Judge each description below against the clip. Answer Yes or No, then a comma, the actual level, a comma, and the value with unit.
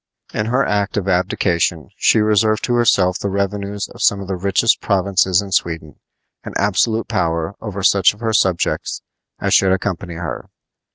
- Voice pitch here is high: No, low, 100 Hz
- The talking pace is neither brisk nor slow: Yes, average, 170 wpm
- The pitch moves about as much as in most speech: No, narrow, 2.3 semitones